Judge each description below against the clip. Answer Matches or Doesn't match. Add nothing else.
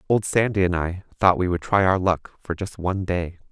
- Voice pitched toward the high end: Doesn't match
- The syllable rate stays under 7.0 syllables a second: Matches